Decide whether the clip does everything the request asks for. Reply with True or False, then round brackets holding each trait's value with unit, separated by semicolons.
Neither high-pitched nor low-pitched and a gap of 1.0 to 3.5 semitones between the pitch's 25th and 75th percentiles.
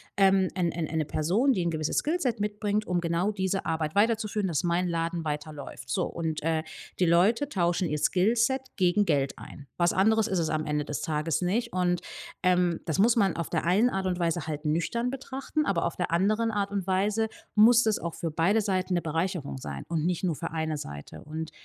False (180 Hz; 4.3 semitones)